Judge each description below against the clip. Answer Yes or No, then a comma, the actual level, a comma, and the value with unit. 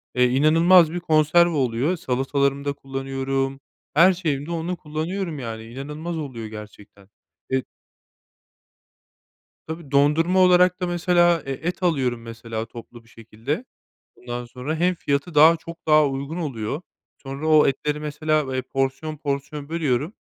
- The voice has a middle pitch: Yes, medium, 145 Hz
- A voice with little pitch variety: No, average, 3.8 semitones